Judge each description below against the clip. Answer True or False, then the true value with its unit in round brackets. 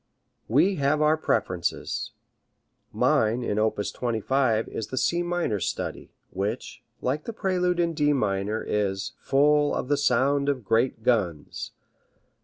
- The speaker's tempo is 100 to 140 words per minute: True (135 wpm)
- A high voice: False (130 Hz)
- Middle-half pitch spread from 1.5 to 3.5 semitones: False (5.6 semitones)